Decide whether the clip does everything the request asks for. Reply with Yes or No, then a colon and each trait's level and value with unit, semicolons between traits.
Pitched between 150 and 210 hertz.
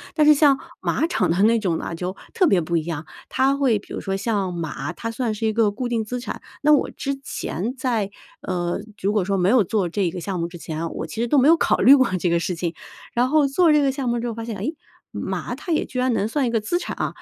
No: high, 225 Hz